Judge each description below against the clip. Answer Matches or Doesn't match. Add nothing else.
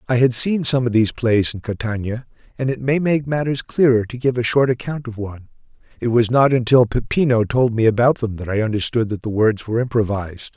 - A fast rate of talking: Matches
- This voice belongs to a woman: Doesn't match